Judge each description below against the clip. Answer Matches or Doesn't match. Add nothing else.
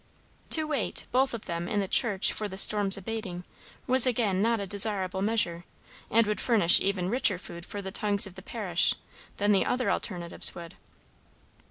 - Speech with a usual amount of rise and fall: Matches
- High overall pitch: Matches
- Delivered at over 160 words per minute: Matches